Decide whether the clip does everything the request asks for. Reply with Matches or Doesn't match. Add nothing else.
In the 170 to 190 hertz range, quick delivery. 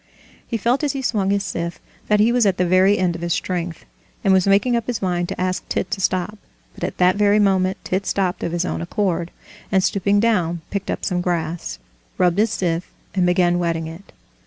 Matches